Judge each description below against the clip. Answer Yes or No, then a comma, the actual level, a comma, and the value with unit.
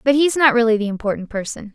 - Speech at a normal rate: No, fast, 240 wpm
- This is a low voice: No, high, 235 Hz